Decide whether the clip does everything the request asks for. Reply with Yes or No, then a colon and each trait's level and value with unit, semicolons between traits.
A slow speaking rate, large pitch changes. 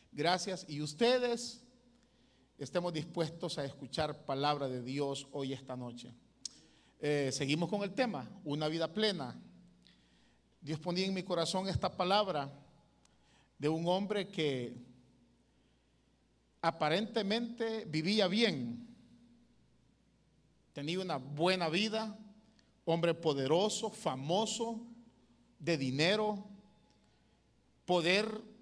Yes: slow, 95 wpm; wide, 7.0 semitones